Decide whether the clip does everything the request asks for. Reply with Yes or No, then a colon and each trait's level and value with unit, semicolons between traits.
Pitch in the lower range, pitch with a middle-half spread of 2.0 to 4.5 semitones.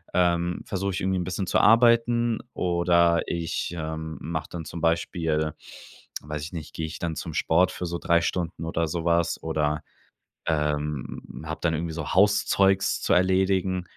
Yes: very low, 85 Hz; narrow, 2.6 semitones